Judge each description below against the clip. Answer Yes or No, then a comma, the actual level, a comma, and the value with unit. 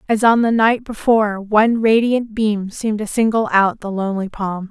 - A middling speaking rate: Yes, average, 190 wpm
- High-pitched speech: Yes, high, 215 Hz